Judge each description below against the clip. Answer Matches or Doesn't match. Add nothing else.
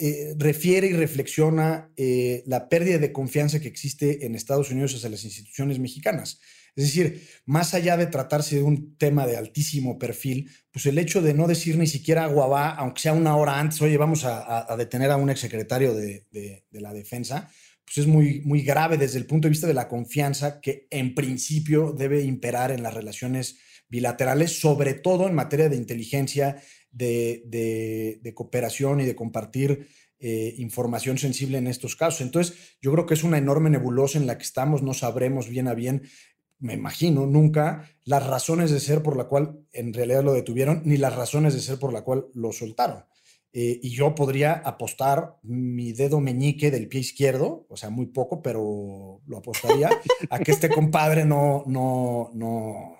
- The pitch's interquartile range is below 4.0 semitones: Matches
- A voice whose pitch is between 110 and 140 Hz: Matches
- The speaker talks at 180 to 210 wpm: Matches